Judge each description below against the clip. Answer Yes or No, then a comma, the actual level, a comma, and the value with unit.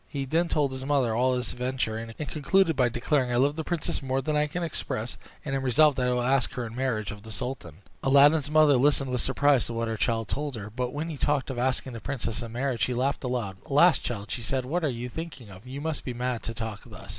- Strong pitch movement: No, average, 3.5 semitones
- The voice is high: No, low, 130 Hz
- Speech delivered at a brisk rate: Yes, fast, 260 wpm